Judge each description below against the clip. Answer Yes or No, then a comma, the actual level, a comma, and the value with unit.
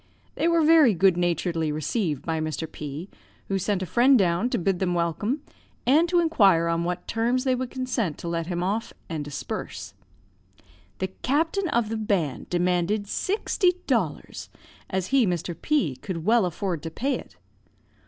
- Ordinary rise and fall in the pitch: No, wide, 6.8 semitones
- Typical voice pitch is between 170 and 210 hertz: Yes, high, 190 Hz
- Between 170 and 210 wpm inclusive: Yes, average, 175 wpm